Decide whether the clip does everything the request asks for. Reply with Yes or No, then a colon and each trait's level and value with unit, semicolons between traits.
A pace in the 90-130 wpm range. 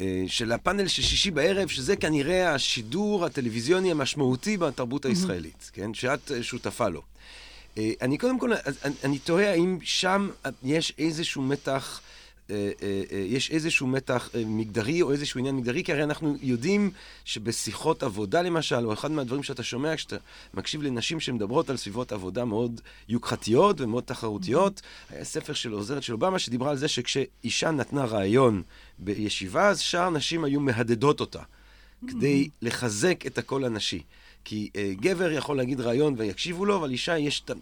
No: average, 145 wpm